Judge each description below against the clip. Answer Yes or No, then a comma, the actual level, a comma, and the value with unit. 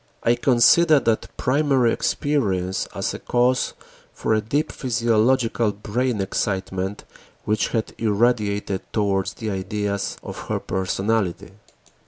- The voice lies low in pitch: Yes, low, 110 Hz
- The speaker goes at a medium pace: No, slow, 110 wpm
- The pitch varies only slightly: No, average, 3.5 semitones